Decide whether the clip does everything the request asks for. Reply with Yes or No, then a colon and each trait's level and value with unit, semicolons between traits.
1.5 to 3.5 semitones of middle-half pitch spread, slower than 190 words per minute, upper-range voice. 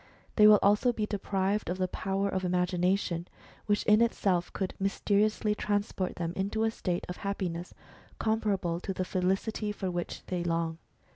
Yes: average, 2.7 semitones; average, 160 wpm; high, 195 Hz